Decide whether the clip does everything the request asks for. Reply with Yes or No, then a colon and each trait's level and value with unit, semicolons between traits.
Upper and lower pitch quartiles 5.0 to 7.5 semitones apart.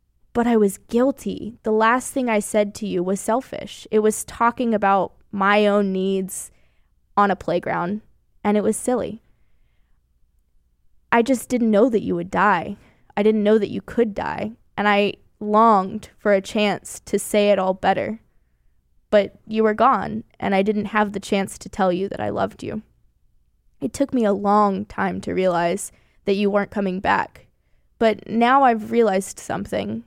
No: narrow, 2.6 semitones